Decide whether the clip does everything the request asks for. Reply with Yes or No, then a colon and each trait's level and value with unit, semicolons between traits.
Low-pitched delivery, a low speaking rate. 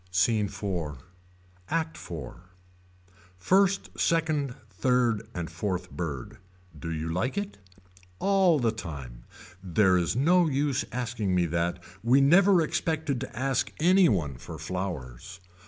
Yes: low, 110 Hz; slow, 125 wpm